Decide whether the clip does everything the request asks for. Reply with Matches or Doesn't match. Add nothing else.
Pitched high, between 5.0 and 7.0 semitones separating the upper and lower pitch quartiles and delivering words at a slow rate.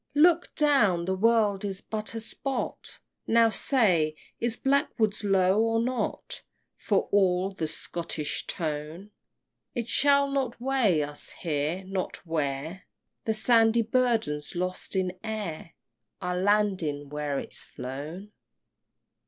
Matches